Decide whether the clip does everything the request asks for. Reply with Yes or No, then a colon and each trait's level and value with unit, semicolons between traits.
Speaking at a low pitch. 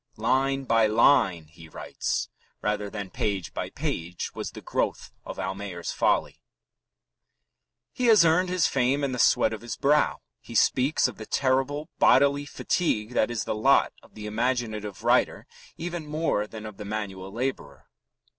Yes: low, 115 Hz